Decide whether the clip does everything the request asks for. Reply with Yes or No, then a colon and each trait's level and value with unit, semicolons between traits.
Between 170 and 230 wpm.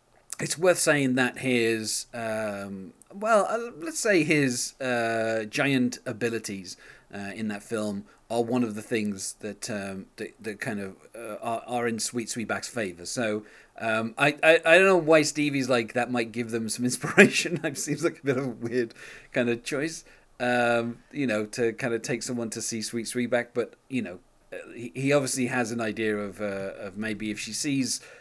Yes: average, 195 wpm